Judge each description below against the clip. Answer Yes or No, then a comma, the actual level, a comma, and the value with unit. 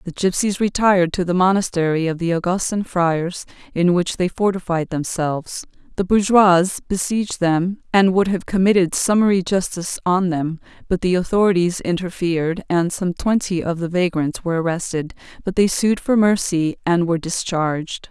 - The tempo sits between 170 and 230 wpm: No, average, 155 wpm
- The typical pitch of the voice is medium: Yes, medium, 180 Hz